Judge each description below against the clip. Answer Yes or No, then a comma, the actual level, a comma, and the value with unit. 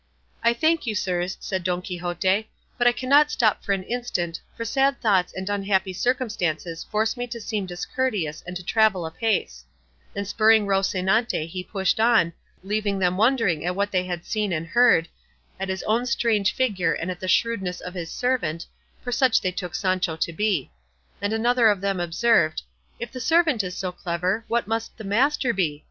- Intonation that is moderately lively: Yes, average, 4.3 semitones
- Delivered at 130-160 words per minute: No, average, 190 wpm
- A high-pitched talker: Yes, high, 200 Hz